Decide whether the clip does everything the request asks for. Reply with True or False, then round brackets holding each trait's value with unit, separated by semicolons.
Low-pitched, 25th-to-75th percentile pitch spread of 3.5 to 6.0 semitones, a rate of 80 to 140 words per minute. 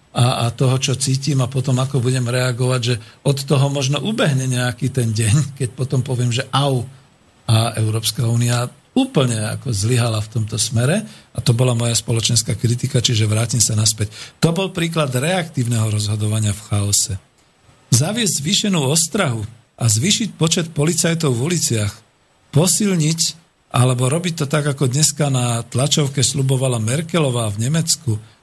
False (130 Hz; 4.1 semitones; 150 wpm)